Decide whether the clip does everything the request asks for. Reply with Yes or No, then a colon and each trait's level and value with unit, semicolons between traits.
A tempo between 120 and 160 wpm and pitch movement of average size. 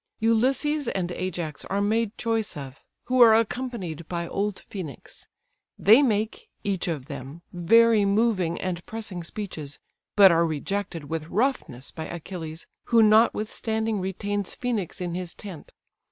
Yes: average, 140 wpm; average, 4.8 semitones